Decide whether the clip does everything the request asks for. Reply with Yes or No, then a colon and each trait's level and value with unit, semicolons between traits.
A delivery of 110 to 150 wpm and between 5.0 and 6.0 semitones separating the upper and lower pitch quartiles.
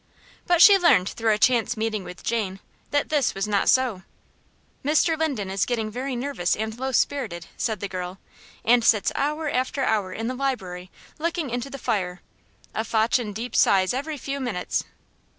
No: average, 175 wpm; average, 5.3 semitones